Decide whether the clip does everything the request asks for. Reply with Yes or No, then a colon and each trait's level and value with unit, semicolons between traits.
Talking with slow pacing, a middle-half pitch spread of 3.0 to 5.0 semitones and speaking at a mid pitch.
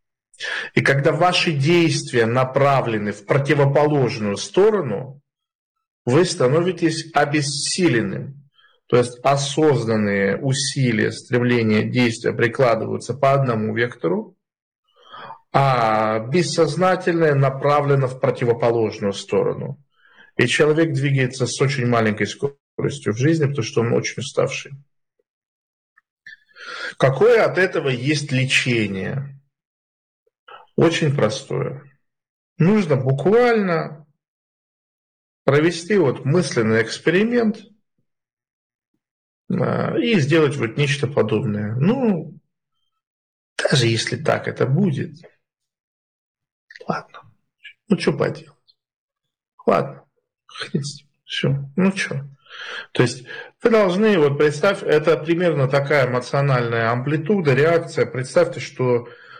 No: slow, 90 wpm; wide, 5.5 semitones; medium, 145 Hz